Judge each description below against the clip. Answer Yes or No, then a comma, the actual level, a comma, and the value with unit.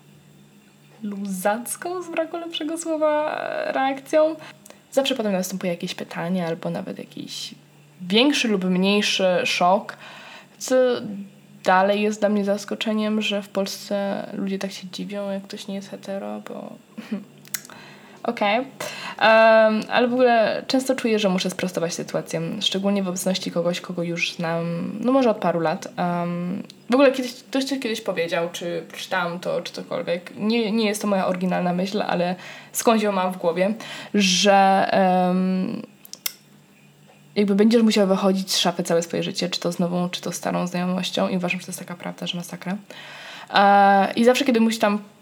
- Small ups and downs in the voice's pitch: No, average, 3.5 semitones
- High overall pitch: Yes, high, 200 Hz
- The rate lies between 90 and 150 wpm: No, fast, 160 wpm